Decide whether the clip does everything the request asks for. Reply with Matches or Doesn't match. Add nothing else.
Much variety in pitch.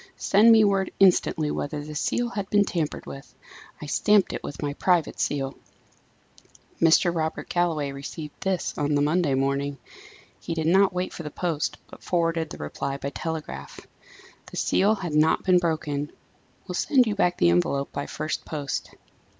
Doesn't match